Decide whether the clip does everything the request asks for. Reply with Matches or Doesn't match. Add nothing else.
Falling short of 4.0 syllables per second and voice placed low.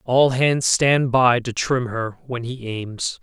Matches